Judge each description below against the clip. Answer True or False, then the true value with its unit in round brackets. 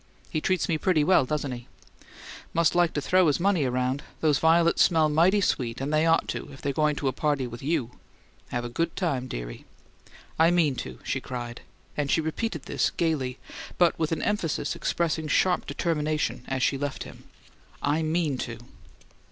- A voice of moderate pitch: True (155 Hz)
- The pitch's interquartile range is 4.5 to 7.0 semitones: False (3.9 semitones)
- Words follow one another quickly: False (185 wpm)